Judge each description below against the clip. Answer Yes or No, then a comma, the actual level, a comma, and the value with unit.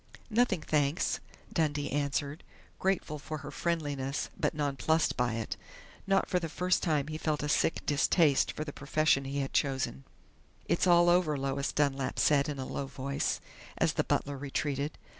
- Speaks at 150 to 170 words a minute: Yes, average, 165 wpm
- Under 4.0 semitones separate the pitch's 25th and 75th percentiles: Yes, narrow, 2.4 semitones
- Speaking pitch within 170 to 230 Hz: No, medium, 145 Hz